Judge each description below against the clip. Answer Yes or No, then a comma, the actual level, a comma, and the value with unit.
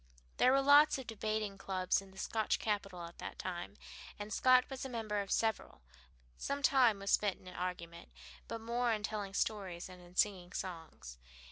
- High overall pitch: Yes, high, 205 Hz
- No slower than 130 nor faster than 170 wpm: No, average, 180 wpm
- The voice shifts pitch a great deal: No, average, 3.9 semitones